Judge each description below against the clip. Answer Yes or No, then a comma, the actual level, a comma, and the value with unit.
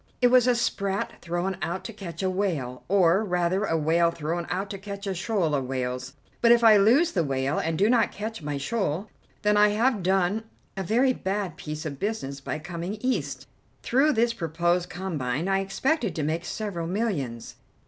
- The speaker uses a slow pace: No, average, 190 wpm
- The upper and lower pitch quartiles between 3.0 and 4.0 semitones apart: No, average, 4.6 semitones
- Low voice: No, high, 190 Hz